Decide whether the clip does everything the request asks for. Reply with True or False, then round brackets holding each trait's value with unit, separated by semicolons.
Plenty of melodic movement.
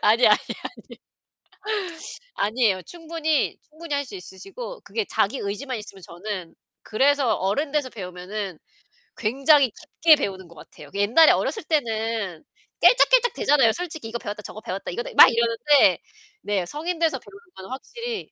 True (7.4 semitones)